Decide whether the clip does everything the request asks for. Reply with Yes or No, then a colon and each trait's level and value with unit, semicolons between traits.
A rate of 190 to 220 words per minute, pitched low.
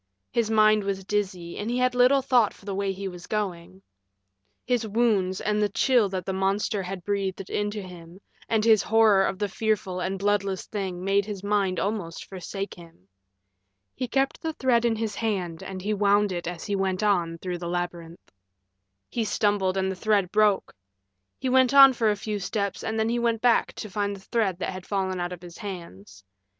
No: average, 200 wpm; high, 200 Hz